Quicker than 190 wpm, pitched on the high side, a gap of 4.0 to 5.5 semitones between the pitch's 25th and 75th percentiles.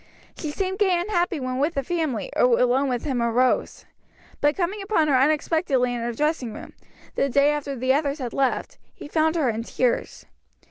Yes: average, 200 wpm; very high, 280 Hz; average, 4.3 semitones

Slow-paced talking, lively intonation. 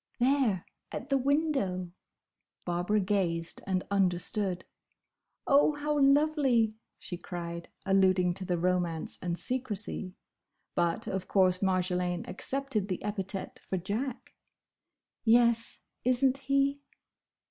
Yes: slow, 110 wpm; wide, 6.3 semitones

